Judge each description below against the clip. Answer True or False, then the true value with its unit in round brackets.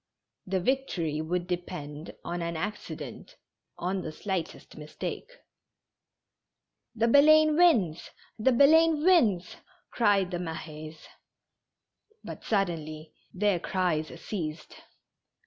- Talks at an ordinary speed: False (100 wpm)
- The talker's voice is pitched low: False (180 Hz)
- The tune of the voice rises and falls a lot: True (6.3 semitones)